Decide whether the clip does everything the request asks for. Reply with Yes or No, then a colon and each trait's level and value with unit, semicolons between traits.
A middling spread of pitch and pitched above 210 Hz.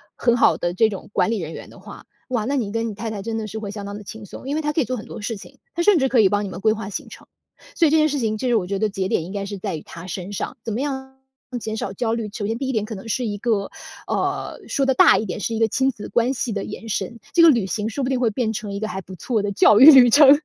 Yes: average, 3.9 semitones; high, 220 Hz